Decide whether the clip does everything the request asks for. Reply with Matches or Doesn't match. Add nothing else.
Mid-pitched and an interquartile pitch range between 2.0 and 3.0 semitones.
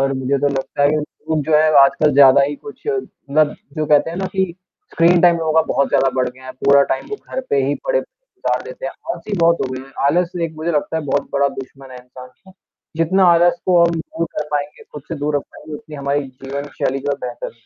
Doesn't match